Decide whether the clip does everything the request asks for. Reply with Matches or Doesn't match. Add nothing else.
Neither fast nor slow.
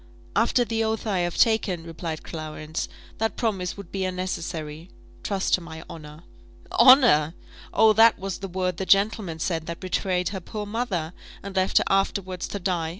Matches